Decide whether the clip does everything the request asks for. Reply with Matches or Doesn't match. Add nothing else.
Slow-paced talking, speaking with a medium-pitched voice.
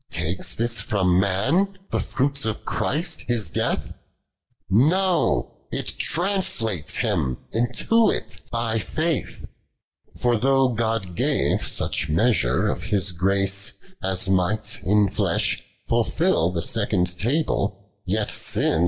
Doesn't match